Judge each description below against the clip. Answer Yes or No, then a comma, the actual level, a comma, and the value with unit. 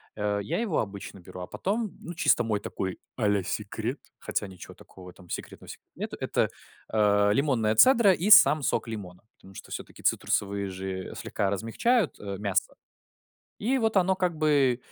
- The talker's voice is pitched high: No, low, 110 Hz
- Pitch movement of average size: No, wide, 8.7 semitones